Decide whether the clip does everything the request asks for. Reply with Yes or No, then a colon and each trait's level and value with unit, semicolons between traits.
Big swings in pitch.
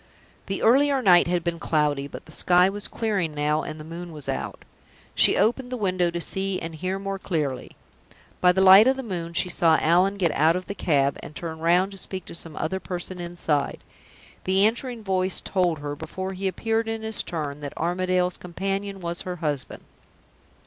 No: average, 3.2 semitones